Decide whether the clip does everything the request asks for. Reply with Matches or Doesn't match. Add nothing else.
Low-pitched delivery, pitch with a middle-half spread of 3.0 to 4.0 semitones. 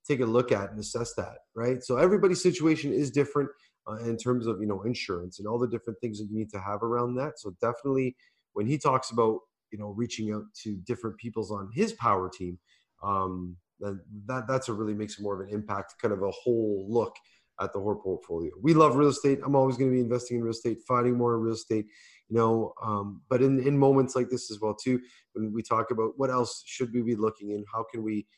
Matches